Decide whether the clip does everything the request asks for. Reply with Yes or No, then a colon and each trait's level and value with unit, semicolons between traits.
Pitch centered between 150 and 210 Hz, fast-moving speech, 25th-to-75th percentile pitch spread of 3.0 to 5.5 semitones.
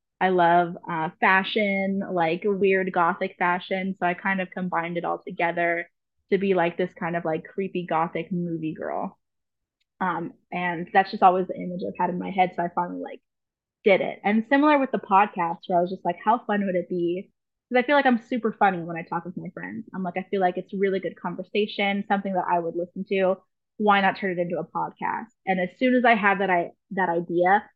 No: medium, 185 Hz; fast, 225 wpm; narrow, 2.4 semitones